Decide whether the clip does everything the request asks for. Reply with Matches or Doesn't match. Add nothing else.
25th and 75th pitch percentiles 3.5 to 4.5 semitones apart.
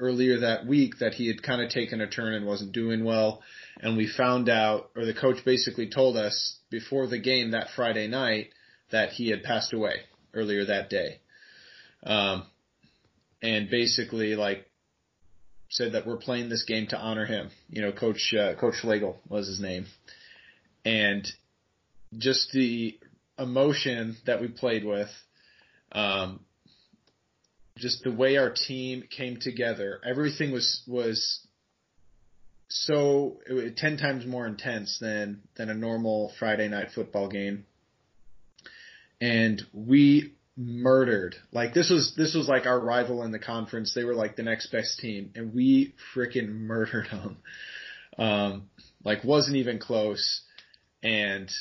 Doesn't match